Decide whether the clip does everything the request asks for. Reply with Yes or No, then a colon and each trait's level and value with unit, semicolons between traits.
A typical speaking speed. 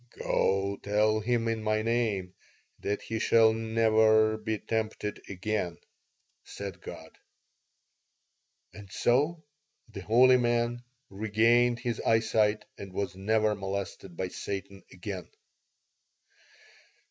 No: slow, 105 wpm